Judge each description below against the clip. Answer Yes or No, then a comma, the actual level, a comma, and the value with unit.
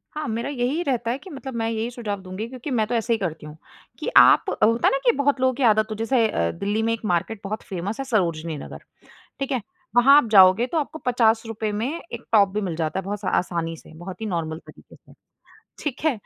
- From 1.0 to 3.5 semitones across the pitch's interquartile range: No, average, 4.7 semitones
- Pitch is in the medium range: No, high, 225 Hz